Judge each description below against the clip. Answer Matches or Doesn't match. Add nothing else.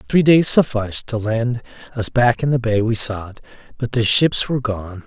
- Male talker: Matches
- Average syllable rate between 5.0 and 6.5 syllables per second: Doesn't match